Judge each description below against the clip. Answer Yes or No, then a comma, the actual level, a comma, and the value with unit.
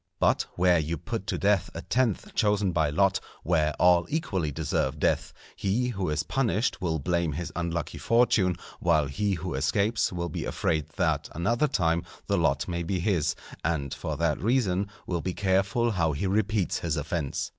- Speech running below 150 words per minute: No, average, 175 wpm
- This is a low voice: Yes, very low, 90 Hz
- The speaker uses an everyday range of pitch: Yes, average, 4.1 semitones